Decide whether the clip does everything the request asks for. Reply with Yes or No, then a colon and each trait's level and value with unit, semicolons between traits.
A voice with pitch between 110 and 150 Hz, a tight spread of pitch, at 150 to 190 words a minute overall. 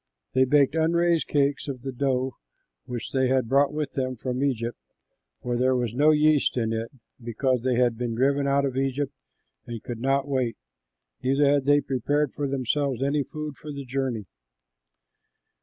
Yes: low, 135 Hz; narrow, 2.3 semitones; average, 175 wpm